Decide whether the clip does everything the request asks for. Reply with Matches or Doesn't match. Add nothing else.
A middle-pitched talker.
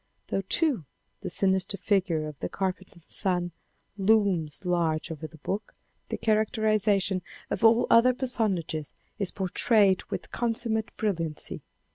Doesn't match